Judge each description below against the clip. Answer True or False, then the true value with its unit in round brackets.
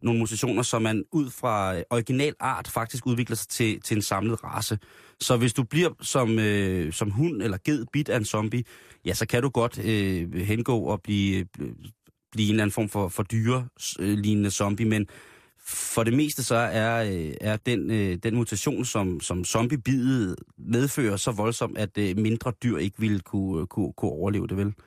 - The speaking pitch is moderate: False (110 Hz)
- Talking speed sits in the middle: True (190 wpm)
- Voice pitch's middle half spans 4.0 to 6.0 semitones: False (3.3 semitones)